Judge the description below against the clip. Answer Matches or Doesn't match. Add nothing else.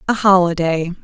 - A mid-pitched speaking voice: Matches